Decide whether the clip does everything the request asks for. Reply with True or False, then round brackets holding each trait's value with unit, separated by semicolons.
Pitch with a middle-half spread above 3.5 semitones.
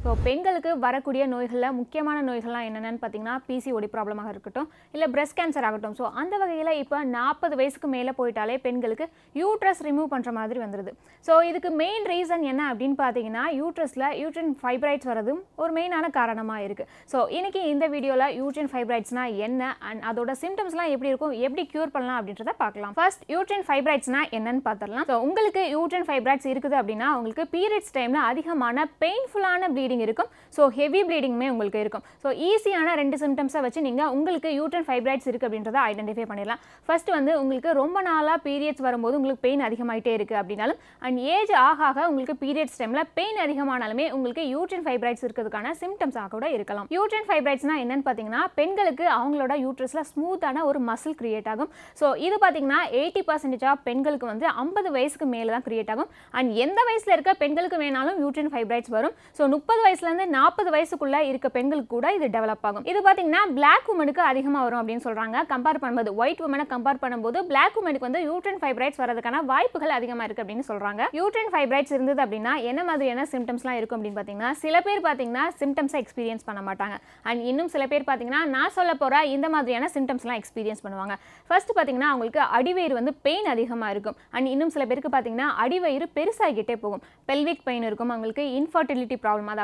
True (4.8 semitones)